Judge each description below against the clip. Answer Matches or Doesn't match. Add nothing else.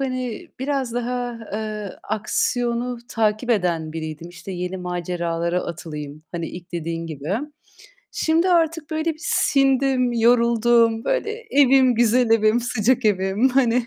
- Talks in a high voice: Matches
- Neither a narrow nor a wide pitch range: Doesn't match